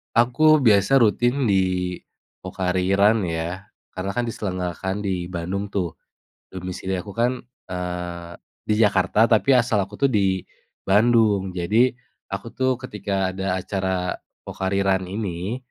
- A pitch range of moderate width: Yes, average, 3.2 semitones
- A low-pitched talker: Yes, very low, 95 Hz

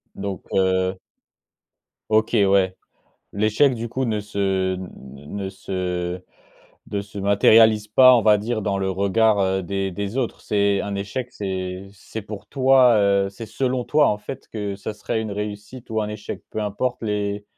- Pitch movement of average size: No, narrow, 2.2 semitones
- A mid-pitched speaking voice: No, low, 105 Hz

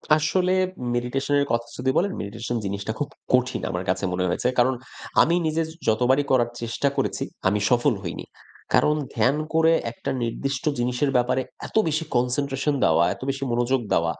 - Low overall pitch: Yes, low, 125 Hz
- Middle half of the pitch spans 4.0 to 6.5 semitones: No, average, 3.3 semitones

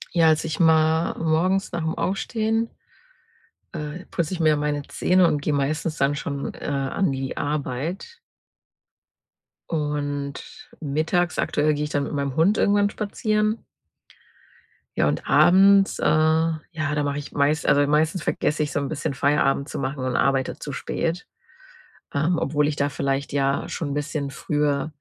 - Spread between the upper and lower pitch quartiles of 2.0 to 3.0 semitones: Yes, average, 2.7 semitones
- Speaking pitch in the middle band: Yes, medium, 150 Hz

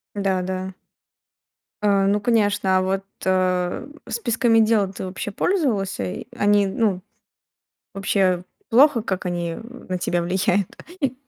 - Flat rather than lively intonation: No, average, 3.1 semitones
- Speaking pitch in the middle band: No, high, 195 Hz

